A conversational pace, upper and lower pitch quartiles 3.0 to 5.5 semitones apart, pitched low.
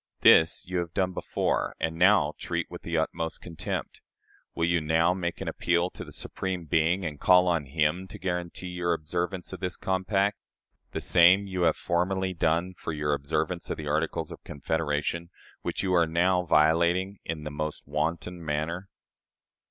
No: average, 175 wpm; narrow, 2.4 semitones; very low, 85 Hz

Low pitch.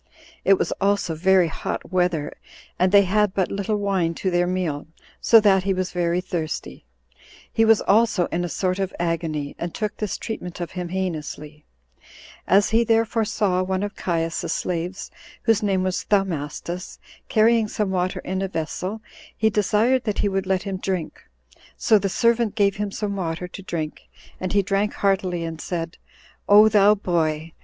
No: high, 190 Hz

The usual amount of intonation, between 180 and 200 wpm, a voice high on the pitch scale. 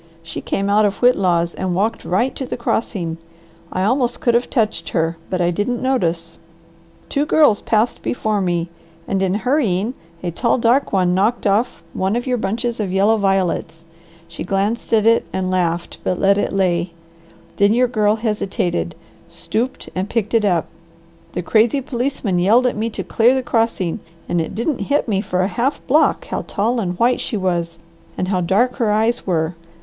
Yes: average, 4.5 semitones; average, 185 wpm; high, 205 Hz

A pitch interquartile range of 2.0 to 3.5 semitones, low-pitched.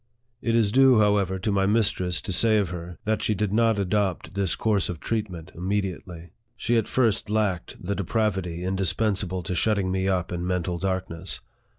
Yes: average, 2.9 semitones; very low, 95 Hz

